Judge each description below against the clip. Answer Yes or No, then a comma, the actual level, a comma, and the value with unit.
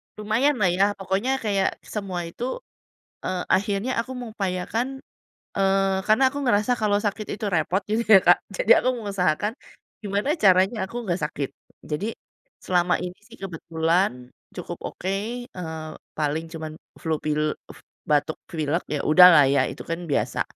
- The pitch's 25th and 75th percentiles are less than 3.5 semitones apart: No, average, 4.4 semitones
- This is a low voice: No, high, 190 Hz